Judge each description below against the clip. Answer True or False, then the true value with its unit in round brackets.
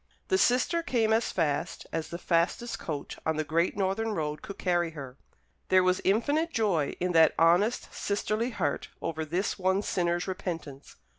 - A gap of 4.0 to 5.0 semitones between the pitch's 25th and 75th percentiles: True (4.7 semitones)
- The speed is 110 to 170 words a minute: True (165 wpm)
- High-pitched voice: False (180 Hz)